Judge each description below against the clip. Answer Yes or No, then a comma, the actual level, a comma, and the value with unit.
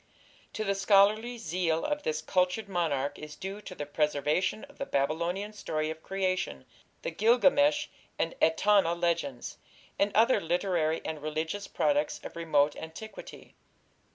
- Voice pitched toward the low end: No, medium, 175 Hz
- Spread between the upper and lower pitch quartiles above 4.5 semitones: Yes, average, 5.0 semitones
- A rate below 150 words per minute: Yes, slow, 135 wpm